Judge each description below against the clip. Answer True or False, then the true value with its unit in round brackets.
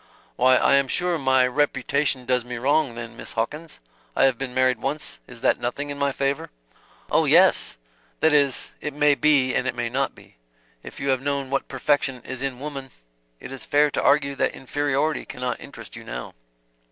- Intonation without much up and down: True (2.3 semitones)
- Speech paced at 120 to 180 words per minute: False (195 wpm)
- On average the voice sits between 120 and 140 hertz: True (135 Hz)